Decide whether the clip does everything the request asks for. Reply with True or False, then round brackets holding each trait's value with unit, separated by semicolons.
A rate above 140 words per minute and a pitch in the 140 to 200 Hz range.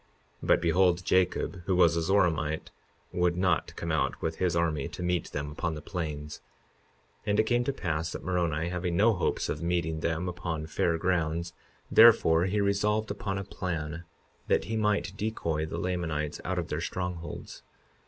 False (175 wpm; 85 Hz)